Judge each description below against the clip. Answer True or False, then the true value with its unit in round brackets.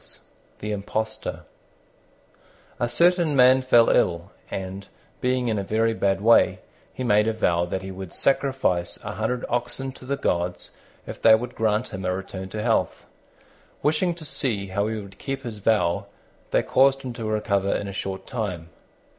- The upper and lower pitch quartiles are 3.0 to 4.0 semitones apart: False (4.6 semitones)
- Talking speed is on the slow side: False (170 wpm)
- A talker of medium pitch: False (110 Hz)